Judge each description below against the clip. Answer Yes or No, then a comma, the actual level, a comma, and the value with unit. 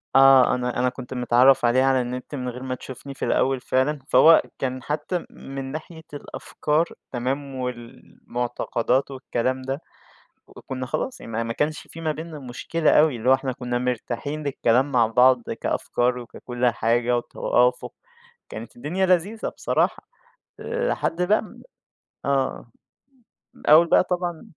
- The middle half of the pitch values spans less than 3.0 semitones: No, average, 3.4 semitones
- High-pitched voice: No, low, 130 Hz